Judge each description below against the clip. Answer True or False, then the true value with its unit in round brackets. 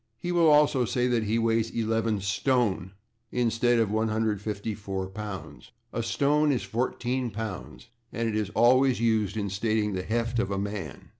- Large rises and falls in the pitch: False (2.6 semitones)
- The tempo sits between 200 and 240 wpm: False (160 wpm)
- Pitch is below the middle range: True (115 Hz)